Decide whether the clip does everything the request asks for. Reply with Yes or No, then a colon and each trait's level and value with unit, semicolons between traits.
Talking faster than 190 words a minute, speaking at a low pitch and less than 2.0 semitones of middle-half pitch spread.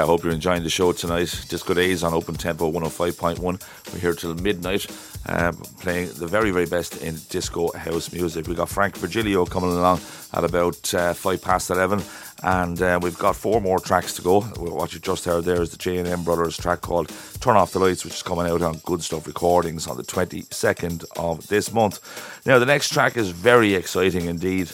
Yes: fast, 205 wpm; very low, 90 Hz; narrow, 1.6 semitones